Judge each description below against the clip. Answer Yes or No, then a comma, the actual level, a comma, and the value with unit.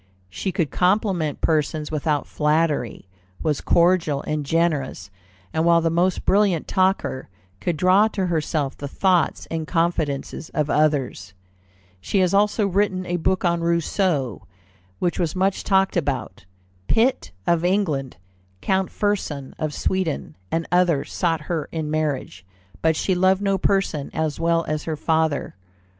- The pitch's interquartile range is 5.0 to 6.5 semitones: No, average, 3.6 semitones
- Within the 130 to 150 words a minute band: Yes, average, 145 wpm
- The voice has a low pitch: No, medium, 165 Hz